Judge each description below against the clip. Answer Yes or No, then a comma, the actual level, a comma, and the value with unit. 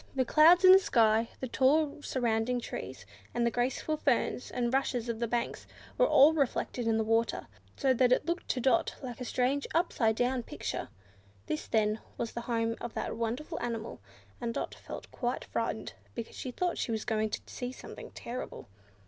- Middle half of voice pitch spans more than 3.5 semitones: No, average, 2.8 semitones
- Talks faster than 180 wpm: Yes, average, 190 wpm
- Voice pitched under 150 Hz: No, high, 245 Hz